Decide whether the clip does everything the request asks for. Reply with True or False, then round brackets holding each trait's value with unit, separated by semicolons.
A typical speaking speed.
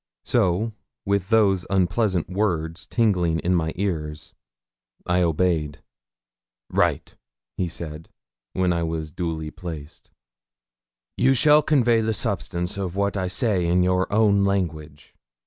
False (125 wpm)